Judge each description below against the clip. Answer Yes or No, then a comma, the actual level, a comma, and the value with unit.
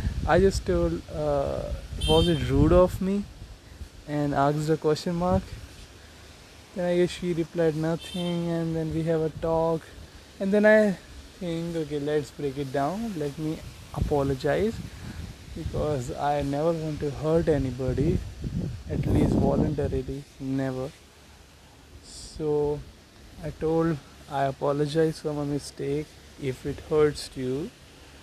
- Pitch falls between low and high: Yes, medium, 145 Hz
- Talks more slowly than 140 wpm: Yes, average, 130 wpm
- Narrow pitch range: No, average, 4.4 semitones